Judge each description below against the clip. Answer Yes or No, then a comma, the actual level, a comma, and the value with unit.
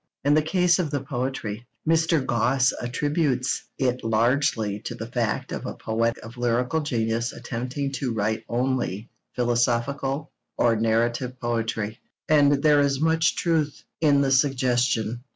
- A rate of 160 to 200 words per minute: No, average, 140 wpm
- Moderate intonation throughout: Yes, average, 3.5 semitones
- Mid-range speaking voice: No, low, 125 Hz